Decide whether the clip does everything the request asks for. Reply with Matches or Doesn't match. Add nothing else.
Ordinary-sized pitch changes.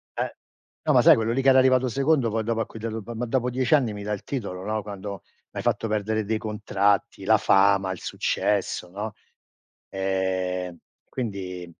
Matches